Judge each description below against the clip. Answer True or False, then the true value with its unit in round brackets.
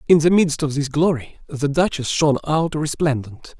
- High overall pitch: False (150 Hz)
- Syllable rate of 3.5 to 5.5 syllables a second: True (5.0 syllables/s)